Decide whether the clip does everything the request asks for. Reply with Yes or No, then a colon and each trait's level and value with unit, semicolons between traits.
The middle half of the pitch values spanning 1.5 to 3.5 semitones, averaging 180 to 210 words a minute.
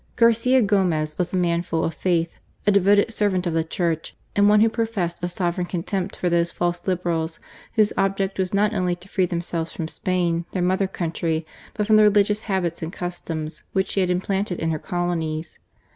Yes: average, 2.8 semitones; average, 195 wpm